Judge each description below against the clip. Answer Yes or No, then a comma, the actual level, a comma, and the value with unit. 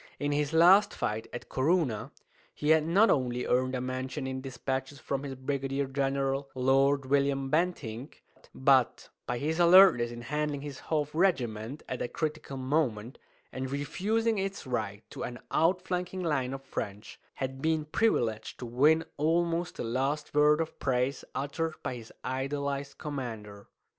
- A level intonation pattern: No, average, 3.4 semitones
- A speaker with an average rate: Yes, average, 155 wpm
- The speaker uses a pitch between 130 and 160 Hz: Yes, medium, 140 Hz